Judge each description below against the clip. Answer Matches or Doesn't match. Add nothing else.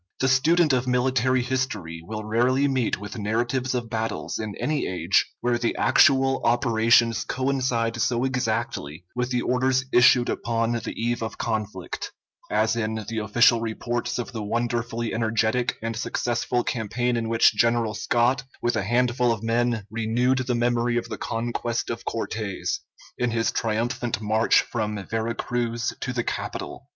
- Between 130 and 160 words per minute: Matches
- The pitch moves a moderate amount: Doesn't match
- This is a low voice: Matches